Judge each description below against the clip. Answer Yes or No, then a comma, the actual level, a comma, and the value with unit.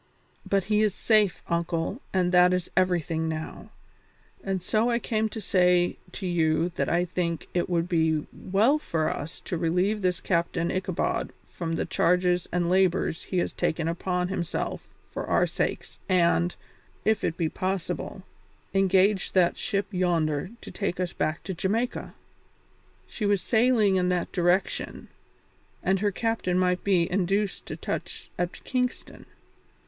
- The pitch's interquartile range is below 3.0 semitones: Yes, narrow, 2.5 semitones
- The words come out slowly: No, average, 155 wpm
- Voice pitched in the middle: Yes, medium, 180 Hz